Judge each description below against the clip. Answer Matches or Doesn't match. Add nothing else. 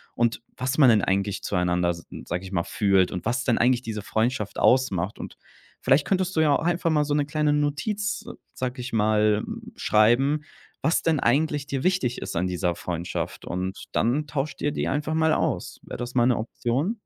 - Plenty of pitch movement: Matches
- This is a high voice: Doesn't match